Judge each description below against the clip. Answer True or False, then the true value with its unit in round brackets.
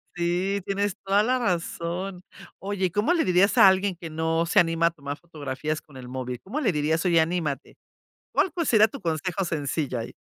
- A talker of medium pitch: True (175 Hz)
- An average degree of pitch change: True (3.9 semitones)